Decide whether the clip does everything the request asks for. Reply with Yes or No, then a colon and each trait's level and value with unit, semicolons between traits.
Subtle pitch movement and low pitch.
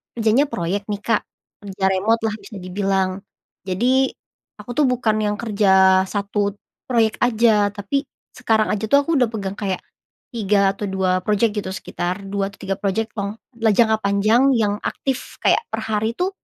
No: narrow, 2.3 semitones; high, 210 Hz